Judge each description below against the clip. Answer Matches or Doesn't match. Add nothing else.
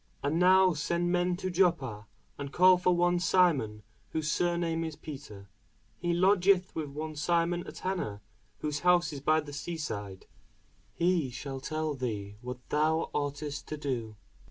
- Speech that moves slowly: Doesn't match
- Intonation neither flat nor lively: Matches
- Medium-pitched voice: Matches